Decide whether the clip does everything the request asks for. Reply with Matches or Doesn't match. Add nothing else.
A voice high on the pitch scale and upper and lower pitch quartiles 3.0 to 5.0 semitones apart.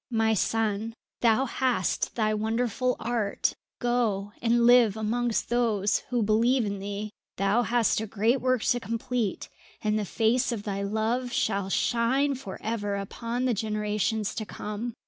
Doesn't match